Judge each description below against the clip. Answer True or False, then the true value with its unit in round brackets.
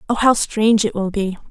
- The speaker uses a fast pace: True (240 wpm)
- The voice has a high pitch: True (210 Hz)